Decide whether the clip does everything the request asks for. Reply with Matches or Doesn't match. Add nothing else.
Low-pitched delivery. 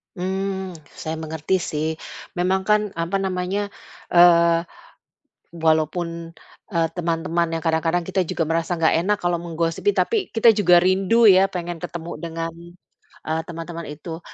Doesn't match